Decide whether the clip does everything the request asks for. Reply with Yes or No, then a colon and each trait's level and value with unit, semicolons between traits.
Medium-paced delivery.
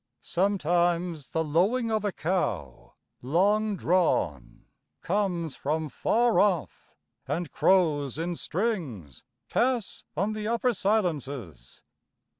No: slow, 100 wpm